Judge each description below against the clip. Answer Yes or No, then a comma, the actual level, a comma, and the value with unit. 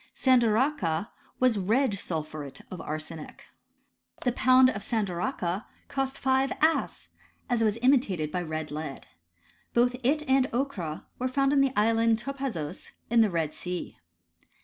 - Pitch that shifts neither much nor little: No, wide, 7.3 semitones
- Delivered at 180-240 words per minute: No, slow, 135 wpm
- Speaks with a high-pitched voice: Yes, high, 225 Hz